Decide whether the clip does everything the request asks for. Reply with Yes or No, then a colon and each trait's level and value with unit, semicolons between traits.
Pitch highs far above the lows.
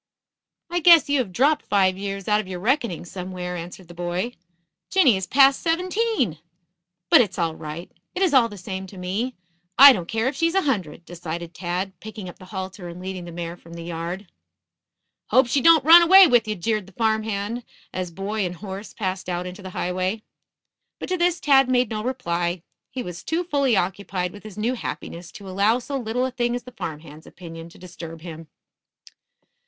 Yes: wide, 6.0 semitones